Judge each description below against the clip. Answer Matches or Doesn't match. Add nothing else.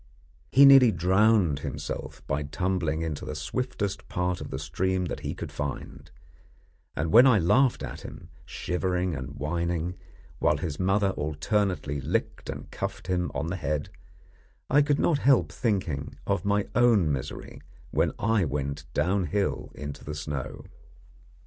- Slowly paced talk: Doesn't match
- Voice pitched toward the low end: Matches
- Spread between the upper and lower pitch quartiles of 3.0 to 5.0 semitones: Doesn't match